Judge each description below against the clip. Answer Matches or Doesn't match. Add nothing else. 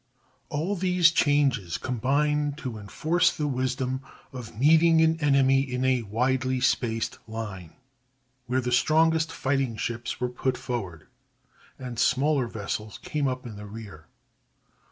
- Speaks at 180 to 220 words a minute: Doesn't match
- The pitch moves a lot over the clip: Doesn't match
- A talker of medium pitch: Doesn't match